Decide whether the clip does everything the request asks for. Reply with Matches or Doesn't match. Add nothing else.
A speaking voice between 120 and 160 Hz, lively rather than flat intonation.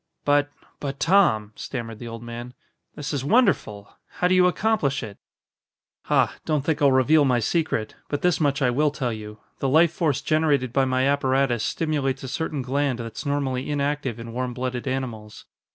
Doesn't match